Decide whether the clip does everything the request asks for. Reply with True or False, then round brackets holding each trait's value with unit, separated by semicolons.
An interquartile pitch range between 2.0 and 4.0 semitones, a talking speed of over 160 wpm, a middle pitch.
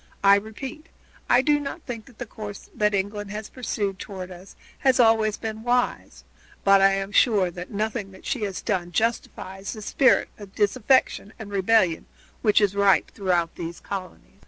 False (2.7 semitones; 175 wpm; 205 Hz)